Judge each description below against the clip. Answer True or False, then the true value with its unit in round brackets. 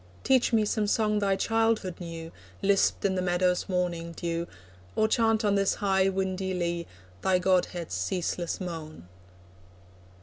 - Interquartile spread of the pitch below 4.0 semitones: True (2.9 semitones)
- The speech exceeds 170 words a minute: False (140 wpm)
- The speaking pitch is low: False (185 Hz)